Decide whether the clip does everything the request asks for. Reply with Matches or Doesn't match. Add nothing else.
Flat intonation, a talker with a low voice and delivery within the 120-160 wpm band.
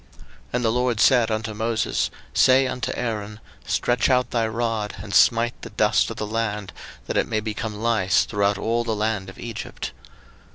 Doesn't match